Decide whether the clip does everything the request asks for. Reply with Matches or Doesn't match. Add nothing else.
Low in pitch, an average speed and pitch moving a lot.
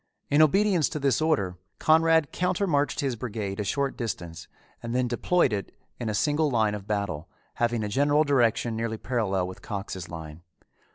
Matches